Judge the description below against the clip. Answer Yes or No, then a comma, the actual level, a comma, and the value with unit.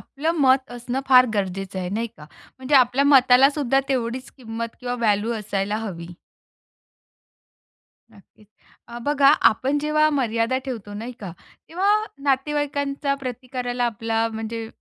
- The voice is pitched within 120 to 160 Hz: No, high, 245 Hz